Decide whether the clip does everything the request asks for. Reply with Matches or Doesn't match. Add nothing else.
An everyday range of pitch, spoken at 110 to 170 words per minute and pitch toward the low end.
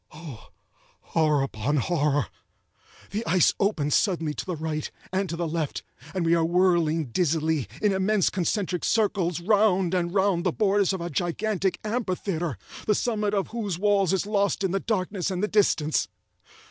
Doesn't match